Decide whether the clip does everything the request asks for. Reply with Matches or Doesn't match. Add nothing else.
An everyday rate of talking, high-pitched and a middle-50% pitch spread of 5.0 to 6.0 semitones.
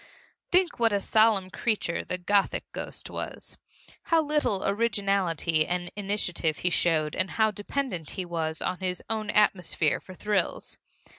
Doesn't match